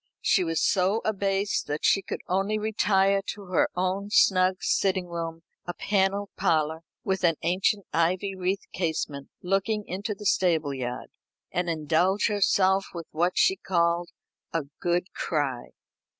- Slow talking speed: No, average, 145 wpm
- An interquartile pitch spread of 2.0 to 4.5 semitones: Yes, average, 2.8 semitones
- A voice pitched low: No, medium, 185 Hz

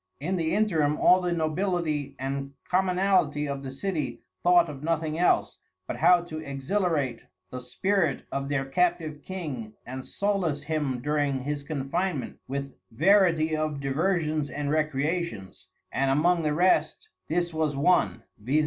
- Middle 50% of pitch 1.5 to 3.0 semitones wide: No, average, 4.1 semitones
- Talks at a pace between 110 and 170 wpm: Yes, average, 145 wpm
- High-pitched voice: No, medium, 155 Hz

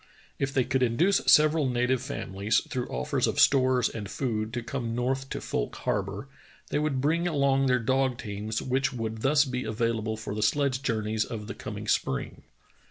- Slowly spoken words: No, average, 180 wpm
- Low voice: Yes, low, 125 Hz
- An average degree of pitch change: Yes, average, 3.5 semitones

